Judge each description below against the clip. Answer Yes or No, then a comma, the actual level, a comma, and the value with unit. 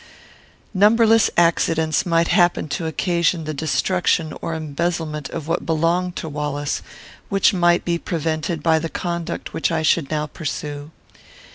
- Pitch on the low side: No, medium, 165 Hz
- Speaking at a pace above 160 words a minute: No, average, 140 wpm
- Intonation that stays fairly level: Yes, narrow, 2.0 semitones